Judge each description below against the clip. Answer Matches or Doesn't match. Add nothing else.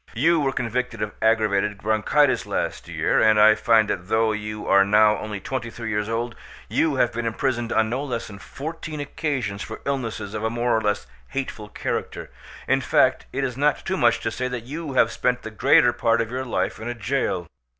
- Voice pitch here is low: Matches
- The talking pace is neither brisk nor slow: Doesn't match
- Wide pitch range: Doesn't match